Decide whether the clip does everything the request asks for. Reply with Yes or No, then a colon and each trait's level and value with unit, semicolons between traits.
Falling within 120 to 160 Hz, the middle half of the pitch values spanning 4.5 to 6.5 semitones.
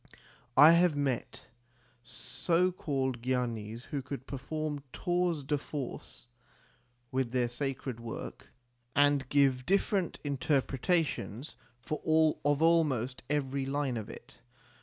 No: medium, 140 Hz; average, 3.4 semitones